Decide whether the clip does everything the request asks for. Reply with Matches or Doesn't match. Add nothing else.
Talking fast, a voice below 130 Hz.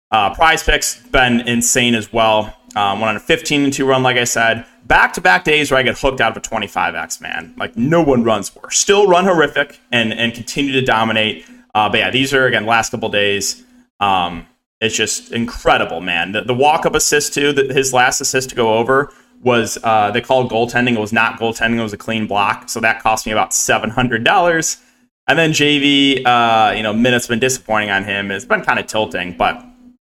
Matches